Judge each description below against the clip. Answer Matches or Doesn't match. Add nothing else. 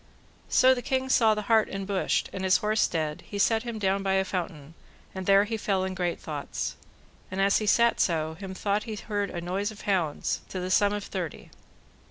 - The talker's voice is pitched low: Doesn't match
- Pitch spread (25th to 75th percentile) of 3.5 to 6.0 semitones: Doesn't match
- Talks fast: Matches